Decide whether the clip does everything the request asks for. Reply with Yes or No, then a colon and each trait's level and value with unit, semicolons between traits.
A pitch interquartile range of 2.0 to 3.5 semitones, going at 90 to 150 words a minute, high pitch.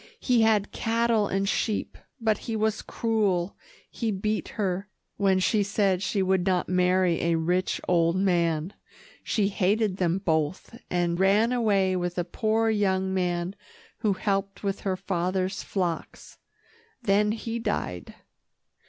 Yes: average, 2.8 semitones; average, 140 wpm; high, 195 Hz